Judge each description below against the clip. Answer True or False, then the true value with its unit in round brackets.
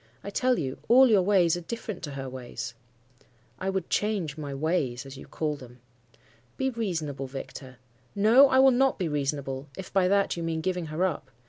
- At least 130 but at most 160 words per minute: False (195 wpm)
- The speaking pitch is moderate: True (165 Hz)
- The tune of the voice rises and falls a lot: True (6.6 semitones)